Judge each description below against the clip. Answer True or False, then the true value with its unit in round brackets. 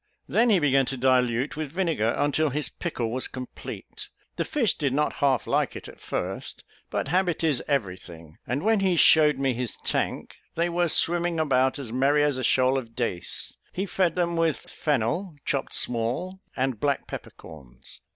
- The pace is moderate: True (180 wpm)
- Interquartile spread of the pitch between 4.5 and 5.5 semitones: True (5.0 semitones)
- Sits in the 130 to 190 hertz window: True (140 Hz)